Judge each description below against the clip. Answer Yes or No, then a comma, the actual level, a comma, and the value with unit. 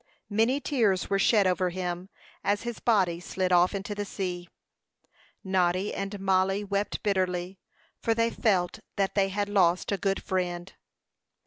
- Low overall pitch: No, high, 195 Hz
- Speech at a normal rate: Yes, average, 150 wpm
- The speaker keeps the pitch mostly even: Yes, narrow, 2.0 semitones